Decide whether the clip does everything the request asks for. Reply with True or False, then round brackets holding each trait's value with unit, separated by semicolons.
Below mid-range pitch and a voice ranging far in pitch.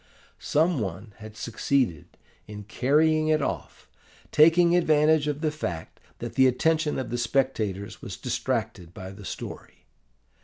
True (130 Hz; 6.7 semitones)